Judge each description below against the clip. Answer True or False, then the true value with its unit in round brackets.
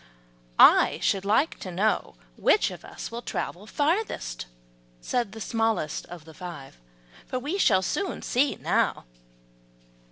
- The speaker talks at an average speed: False (130 wpm)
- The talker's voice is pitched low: False (215 Hz)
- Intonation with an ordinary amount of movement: False (6.3 semitones)